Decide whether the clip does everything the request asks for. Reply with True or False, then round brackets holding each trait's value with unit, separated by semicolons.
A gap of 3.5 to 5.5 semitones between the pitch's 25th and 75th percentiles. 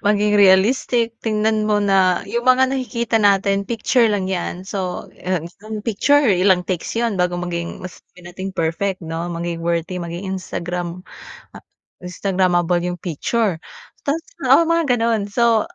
True (3.9 semitones)